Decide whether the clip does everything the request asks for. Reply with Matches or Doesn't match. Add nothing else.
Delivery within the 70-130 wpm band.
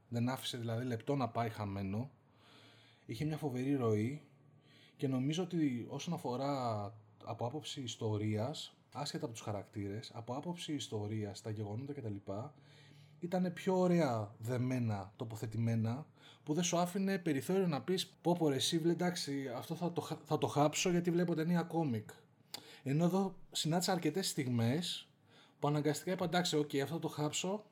Doesn't match